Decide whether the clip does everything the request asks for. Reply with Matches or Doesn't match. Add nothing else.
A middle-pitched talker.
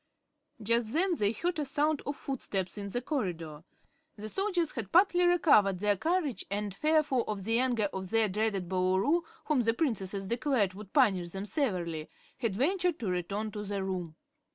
Doesn't match